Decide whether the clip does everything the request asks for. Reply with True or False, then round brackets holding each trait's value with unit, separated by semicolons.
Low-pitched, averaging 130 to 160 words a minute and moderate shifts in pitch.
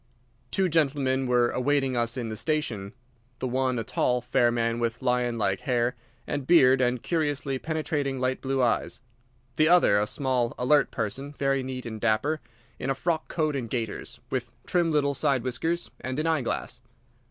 False (130 Hz; 175 wpm; 3.3 semitones)